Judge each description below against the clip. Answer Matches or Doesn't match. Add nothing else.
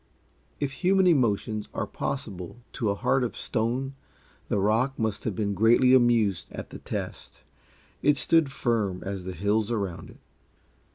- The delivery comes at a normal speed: Matches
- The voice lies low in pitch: Matches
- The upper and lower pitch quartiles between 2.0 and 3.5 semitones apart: Doesn't match